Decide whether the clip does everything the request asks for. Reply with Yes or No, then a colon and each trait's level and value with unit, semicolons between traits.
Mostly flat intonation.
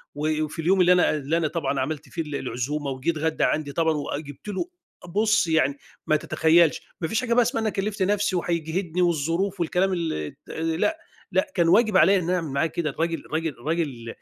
No: average, 3.4 semitones